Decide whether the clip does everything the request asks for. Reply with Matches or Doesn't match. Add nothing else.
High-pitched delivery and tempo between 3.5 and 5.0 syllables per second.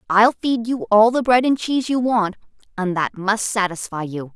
Matches